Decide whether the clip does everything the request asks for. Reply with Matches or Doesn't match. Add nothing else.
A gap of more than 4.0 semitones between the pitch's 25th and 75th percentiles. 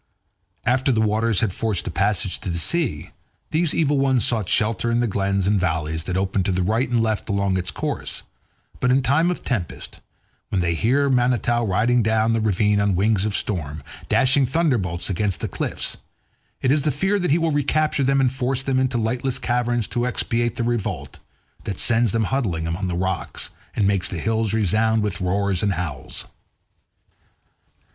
Matches